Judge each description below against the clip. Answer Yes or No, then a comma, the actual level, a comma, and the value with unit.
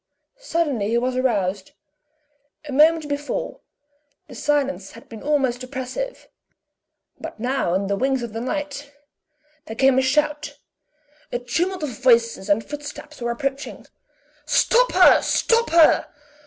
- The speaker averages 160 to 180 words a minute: No, slow, 135 wpm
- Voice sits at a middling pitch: No, very high, 265 Hz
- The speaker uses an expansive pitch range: No, average, 4.0 semitones